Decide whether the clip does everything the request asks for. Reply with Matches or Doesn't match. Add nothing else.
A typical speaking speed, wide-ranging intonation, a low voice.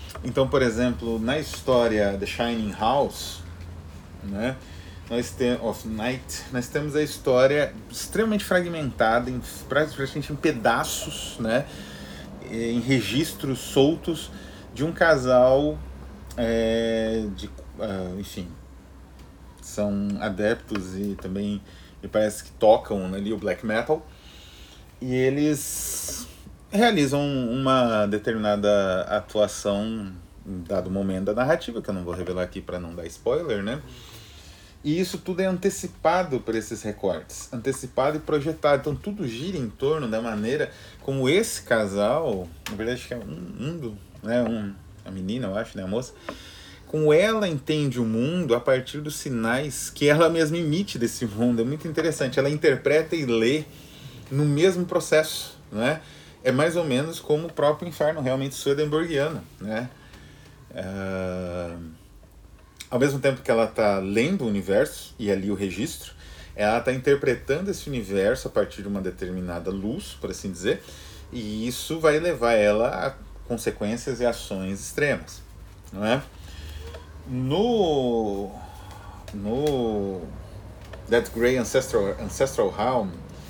Matches